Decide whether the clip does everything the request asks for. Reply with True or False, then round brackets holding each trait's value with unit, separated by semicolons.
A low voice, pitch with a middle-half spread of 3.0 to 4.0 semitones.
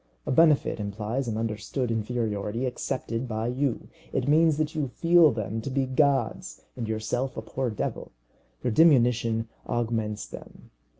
True (120 Hz; 3.6 semitones)